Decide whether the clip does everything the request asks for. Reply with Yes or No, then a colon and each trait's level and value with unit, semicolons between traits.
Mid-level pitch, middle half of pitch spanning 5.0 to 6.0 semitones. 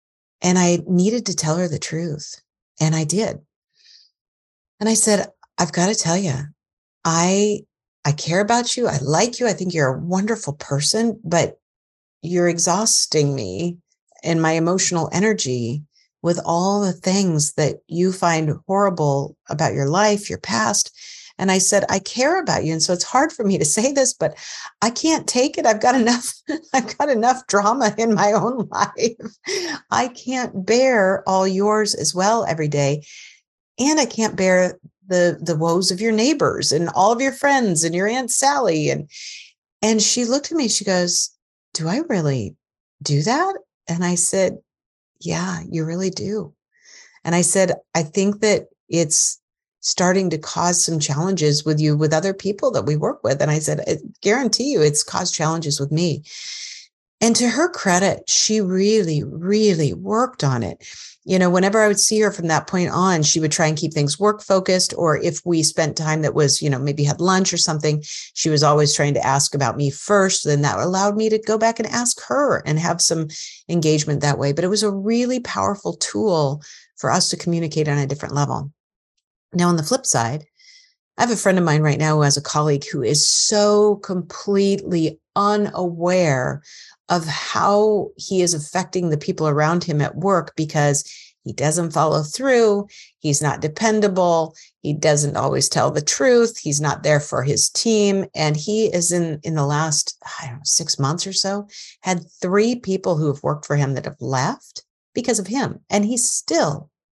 Yes: medium, 180 Hz; wide, 5.6 semitones